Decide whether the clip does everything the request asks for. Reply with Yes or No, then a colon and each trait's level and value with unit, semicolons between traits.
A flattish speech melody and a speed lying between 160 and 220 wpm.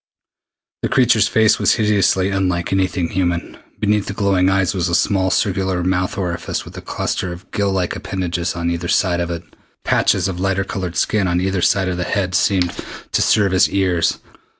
Yes: narrow, 1.8 semitones; average, 190 wpm